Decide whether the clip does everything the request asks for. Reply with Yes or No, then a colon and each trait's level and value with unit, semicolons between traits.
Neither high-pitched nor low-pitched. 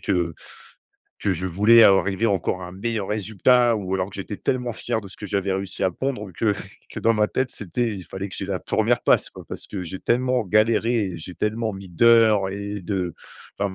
No: low, 100 Hz